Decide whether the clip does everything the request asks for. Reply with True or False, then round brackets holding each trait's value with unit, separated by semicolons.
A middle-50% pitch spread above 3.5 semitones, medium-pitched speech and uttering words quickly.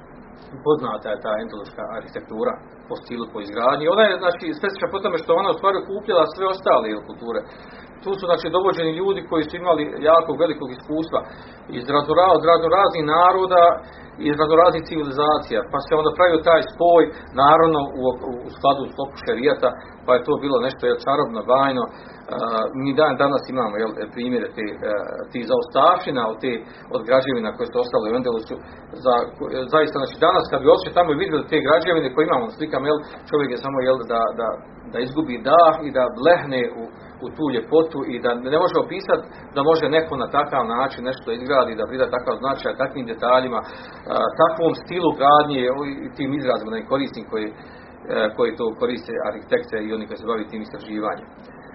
True (4.8 semitones; 155 Hz; 175 wpm)